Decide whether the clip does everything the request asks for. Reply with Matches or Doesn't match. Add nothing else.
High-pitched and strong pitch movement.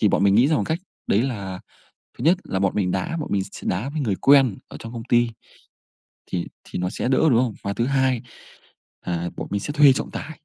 Doesn't match